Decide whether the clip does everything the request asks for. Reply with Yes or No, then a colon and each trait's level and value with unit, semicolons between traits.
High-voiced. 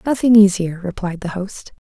Yes: high, 195 Hz